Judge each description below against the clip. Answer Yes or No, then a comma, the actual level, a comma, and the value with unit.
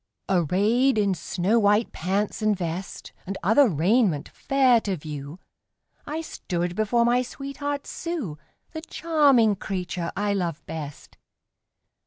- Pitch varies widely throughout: Yes, wide, 6.2 semitones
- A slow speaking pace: Yes, slow, 125 wpm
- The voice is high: Yes, high, 205 Hz